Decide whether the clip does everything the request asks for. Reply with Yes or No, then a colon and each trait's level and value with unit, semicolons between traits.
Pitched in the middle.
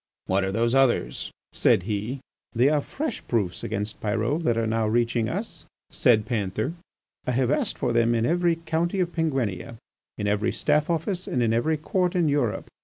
No: low, 120 Hz